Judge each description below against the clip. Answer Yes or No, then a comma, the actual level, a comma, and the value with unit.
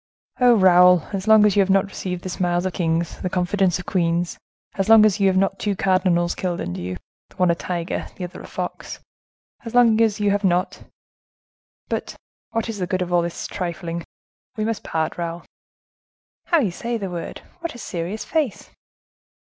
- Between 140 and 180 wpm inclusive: No, average, 195 wpm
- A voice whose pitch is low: No, medium, 185 Hz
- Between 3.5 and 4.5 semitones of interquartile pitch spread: No, average, 3.1 semitones